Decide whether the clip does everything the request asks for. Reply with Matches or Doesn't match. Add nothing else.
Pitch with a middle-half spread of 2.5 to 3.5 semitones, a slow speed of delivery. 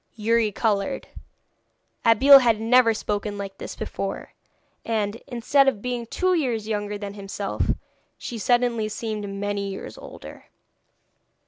Matches